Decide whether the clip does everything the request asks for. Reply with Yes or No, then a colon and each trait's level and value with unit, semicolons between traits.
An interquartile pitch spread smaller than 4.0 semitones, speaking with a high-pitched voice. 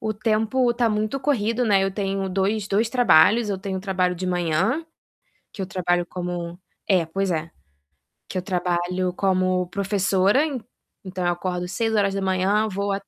Yes: average, 2.7 semitones; high, 195 Hz